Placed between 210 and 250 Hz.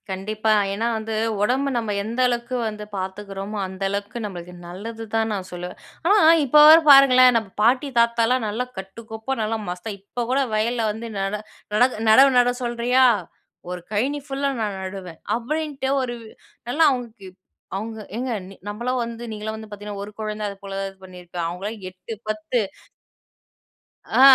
Yes: high, 220 Hz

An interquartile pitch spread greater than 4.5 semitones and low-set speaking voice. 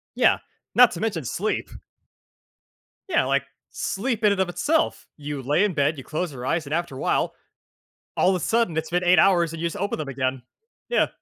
No: wide, 5.4 semitones; medium, 170 Hz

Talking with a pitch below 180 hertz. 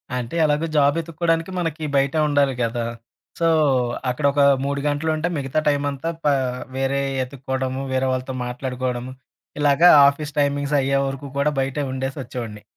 Yes: medium, 140 Hz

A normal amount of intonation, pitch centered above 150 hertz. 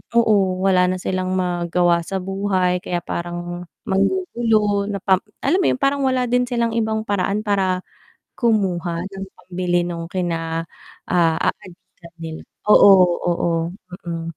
Yes: average, 3.1 semitones; medium, 185 Hz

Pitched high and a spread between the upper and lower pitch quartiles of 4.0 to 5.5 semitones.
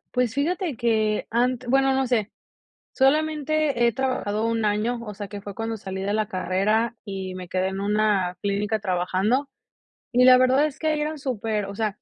Yes: high, 225 Hz; average, 4.4 semitones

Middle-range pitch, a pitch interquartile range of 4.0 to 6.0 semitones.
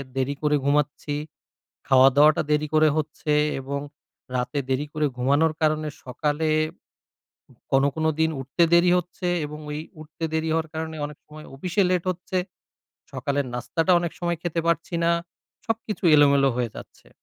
No: medium, 155 Hz; narrow, 2.4 semitones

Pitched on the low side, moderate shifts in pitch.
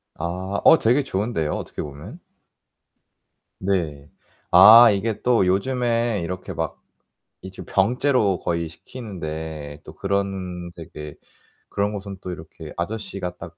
Yes: very low, 95 Hz; average, 4.5 semitones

